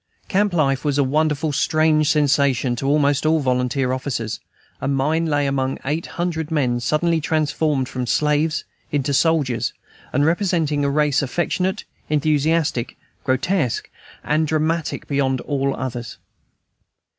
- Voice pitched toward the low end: No, medium, 145 Hz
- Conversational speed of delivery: No, slow, 130 wpm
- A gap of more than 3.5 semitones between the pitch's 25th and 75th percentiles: No, average, 2.9 semitones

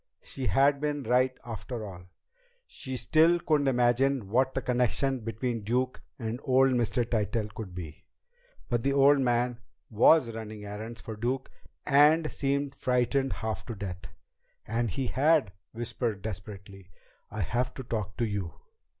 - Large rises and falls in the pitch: No, average, 3.7 semitones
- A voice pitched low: Yes, low, 120 Hz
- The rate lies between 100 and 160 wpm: Yes, average, 150 wpm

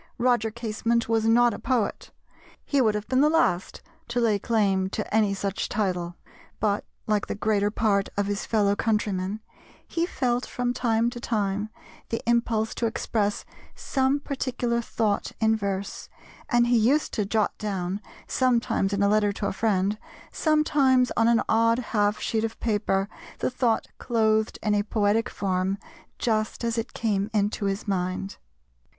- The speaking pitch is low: No, high, 220 Hz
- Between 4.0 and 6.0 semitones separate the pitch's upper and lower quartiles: No, average, 2.7 semitones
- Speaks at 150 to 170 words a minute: Yes, average, 160 wpm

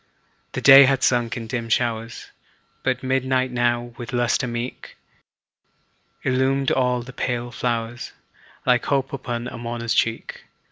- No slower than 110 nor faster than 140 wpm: Yes, slow, 135 wpm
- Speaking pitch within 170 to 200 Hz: No, low, 120 Hz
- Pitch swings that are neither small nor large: No, narrow, 1.6 semitones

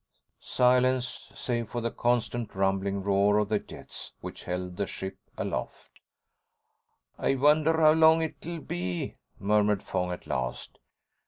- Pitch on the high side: No, low, 105 Hz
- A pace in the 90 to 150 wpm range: Yes, slow, 135 wpm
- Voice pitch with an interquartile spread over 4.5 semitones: Yes, average, 5.0 semitones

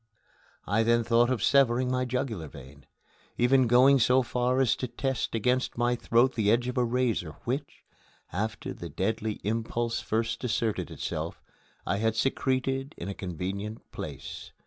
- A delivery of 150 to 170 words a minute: Yes, average, 155 wpm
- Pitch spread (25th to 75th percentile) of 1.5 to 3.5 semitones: Yes, average, 2.7 semitones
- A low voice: Yes, low, 120 Hz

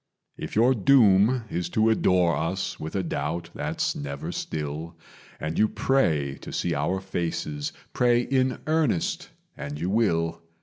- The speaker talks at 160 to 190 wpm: No, average, 145 wpm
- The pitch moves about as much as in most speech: No, wide, 6.1 semitones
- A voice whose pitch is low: Yes, very low, 90 Hz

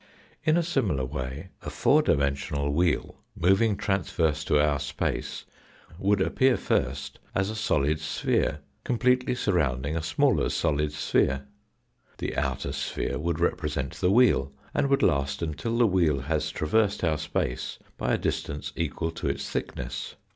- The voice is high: No, very low, 80 Hz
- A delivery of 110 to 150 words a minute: Yes, average, 145 wpm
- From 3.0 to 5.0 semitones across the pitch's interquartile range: No, wide, 5.4 semitones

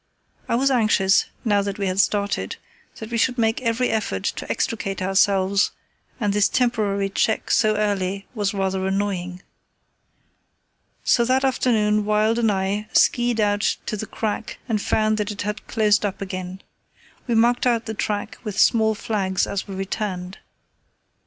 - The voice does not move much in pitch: Yes, narrow, 2.3 semitones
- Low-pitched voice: No, high, 210 Hz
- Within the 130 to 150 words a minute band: No, average, 160 wpm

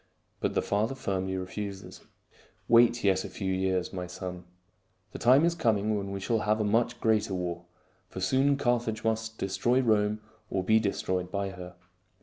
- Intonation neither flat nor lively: Yes, average, 3.2 semitones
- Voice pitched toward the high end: No, low, 105 Hz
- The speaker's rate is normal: Yes, average, 175 wpm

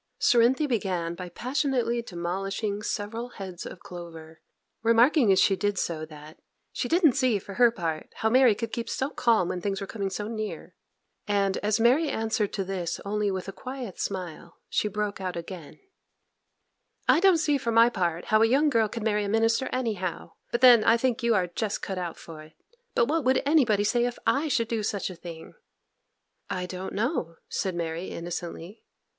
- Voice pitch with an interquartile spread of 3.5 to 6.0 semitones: Yes, average, 4.6 semitones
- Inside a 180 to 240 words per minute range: Yes, average, 190 wpm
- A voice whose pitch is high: Yes, high, 210 Hz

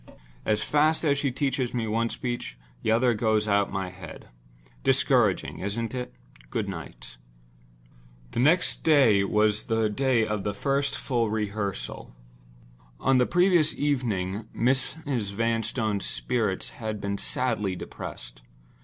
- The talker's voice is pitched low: Yes, low, 115 Hz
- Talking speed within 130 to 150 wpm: Yes, slow, 135 wpm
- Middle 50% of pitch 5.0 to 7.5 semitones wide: No, average, 4.3 semitones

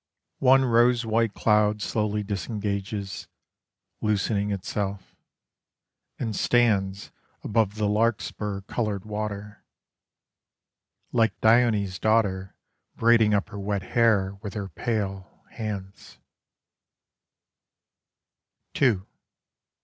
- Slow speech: Yes, slow, 80 wpm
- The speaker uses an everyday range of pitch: No, narrow, 2.1 semitones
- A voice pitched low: Yes, low, 105 Hz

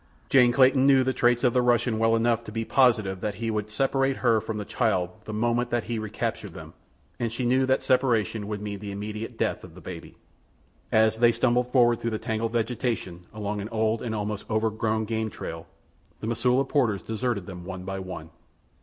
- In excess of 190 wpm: Yes, fast, 205 wpm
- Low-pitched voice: Yes, low, 110 Hz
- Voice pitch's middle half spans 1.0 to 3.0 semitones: Yes, narrow, 2.5 semitones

